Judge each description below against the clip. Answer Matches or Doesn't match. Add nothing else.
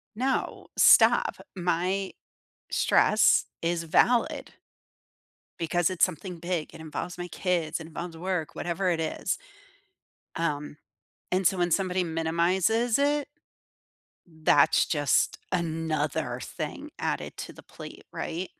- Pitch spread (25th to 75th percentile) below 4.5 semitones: Matches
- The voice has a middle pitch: Matches